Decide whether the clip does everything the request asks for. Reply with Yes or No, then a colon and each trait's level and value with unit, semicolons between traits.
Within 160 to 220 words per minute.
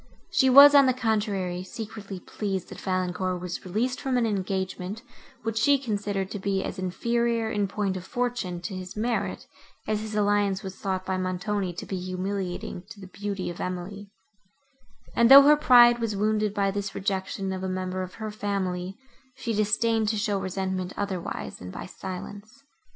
Yes: average, 175 wpm